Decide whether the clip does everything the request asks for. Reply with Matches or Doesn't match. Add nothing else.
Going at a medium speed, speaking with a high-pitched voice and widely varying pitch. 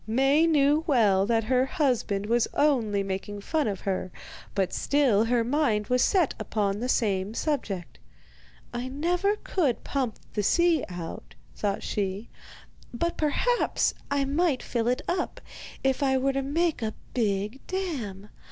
Matches